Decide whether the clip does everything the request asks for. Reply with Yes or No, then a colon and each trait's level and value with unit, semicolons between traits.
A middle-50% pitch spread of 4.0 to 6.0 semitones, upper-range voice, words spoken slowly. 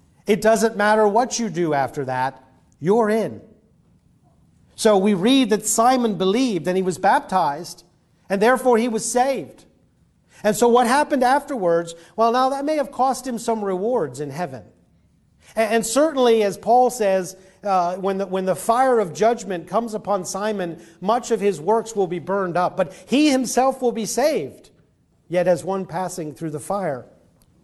No: average, 4.5 semitones; high, 210 Hz; average, 170 wpm